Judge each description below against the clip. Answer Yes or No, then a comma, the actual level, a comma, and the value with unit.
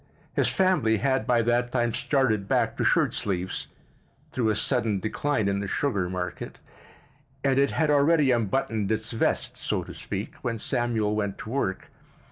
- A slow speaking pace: No, average, 165 wpm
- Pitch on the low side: Yes, low, 115 Hz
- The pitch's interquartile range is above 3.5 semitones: Yes, average, 4.3 semitones